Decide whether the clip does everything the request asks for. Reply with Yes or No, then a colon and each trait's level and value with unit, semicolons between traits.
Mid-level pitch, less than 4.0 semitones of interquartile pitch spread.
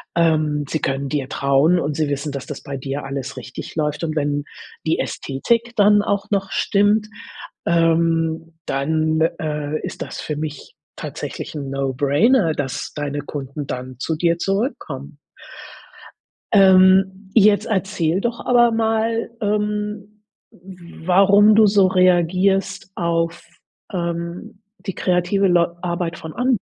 No: medium, 170 Hz; average, 5.1 semitones